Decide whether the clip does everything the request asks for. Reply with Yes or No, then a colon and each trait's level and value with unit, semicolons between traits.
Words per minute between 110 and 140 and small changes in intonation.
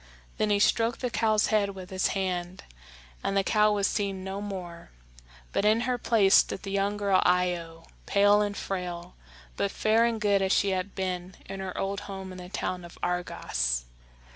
No: average, 190 wpm; narrow, 2.3 semitones